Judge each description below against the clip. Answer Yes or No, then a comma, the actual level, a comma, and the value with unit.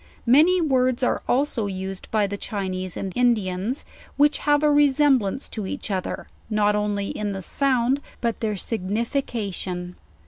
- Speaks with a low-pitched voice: No, high, 220 Hz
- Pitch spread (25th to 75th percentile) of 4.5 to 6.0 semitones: Yes, wide, 5.4 semitones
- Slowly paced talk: No, average, 145 wpm